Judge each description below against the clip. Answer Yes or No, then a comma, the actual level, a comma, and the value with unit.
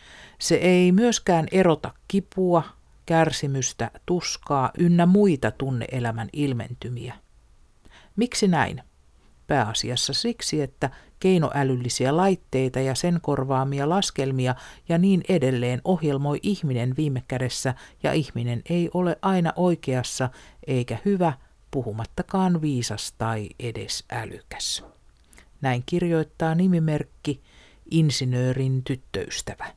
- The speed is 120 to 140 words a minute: No, slow, 95 wpm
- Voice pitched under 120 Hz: No, medium, 140 Hz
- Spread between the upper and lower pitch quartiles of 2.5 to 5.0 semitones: No, wide, 5.5 semitones